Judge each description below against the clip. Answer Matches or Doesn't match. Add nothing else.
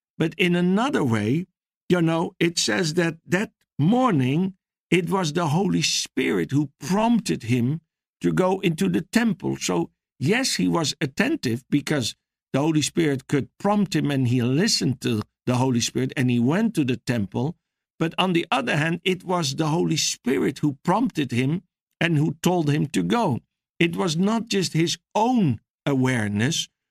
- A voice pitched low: Doesn't match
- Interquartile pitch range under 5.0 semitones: Doesn't match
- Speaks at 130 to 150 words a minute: Doesn't match